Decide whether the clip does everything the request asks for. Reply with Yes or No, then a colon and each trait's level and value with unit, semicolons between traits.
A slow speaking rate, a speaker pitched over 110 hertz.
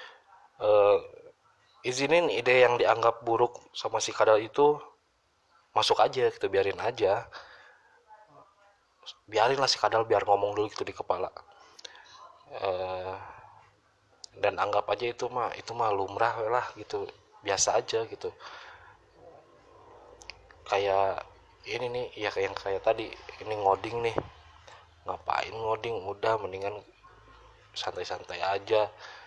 No: average, 115 wpm; low, 135 Hz